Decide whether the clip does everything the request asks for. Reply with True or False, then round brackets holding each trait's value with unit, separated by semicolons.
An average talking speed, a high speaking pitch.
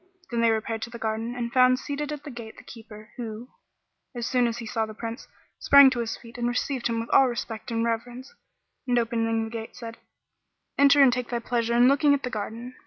False (230 wpm; 235 Hz)